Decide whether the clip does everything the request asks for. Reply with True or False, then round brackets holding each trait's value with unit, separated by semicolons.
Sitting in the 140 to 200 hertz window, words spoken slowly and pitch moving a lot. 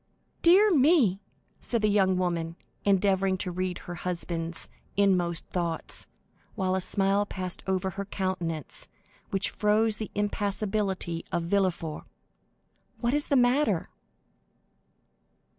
False (190 Hz; 115 wpm; 2.8 semitones)